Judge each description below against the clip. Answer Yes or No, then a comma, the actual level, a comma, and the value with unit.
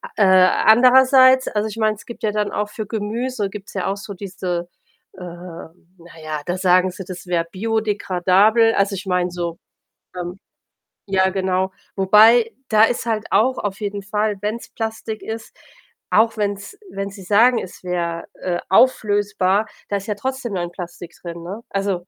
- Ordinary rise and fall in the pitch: Yes, average, 3.1 semitones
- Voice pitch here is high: Yes, high, 200 Hz